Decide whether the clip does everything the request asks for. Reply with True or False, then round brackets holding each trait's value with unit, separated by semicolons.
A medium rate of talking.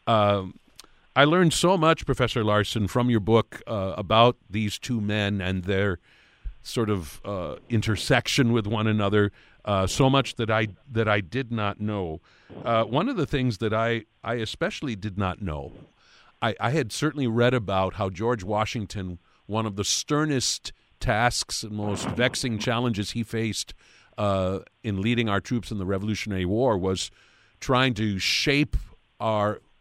True (160 wpm)